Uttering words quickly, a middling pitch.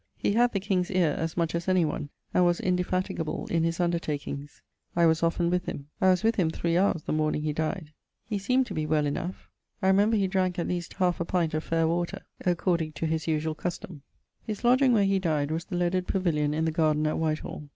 Yes: fast, 225 wpm; medium, 170 Hz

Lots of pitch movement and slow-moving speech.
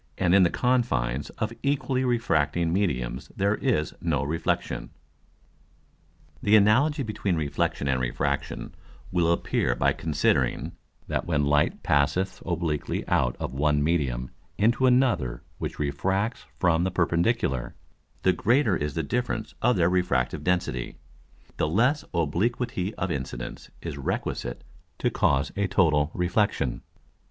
Yes: wide, 6.8 semitones; slow, 130 wpm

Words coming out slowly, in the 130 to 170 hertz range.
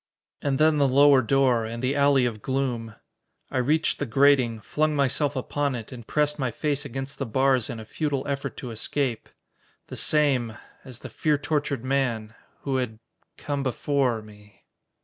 No: average, 170 wpm; low, 135 Hz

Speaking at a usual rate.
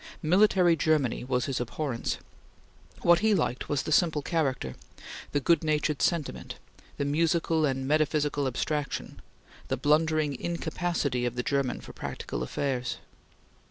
No: slow, 130 wpm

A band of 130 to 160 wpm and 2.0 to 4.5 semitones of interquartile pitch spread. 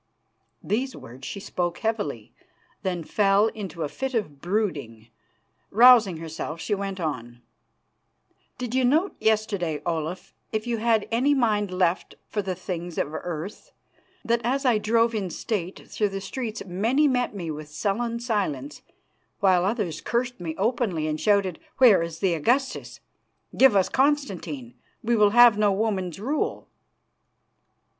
No: average, 145 wpm; wide, 5.5 semitones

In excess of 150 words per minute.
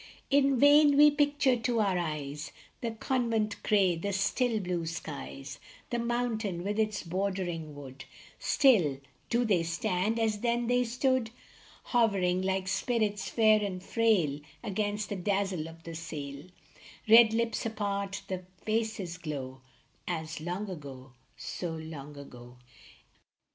No: slow, 135 wpm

